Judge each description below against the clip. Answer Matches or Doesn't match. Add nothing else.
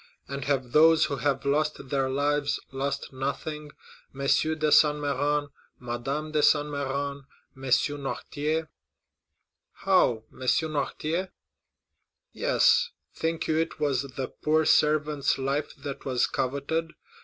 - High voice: Doesn't match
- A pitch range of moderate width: Doesn't match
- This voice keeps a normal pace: Doesn't match